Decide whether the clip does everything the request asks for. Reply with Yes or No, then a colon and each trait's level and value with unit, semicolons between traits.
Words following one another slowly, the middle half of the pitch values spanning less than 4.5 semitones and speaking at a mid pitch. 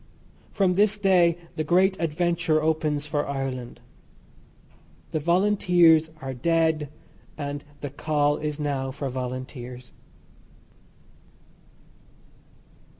Yes: slow, 90 wpm; average, 3.5 semitones; medium, 155 Hz